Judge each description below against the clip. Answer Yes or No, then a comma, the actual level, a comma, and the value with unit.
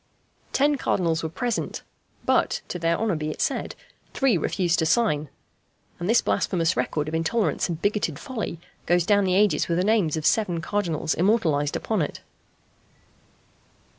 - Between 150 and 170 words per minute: Yes, average, 160 wpm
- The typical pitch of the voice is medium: Yes, medium, 175 Hz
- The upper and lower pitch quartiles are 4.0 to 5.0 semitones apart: Yes, average, 4.6 semitones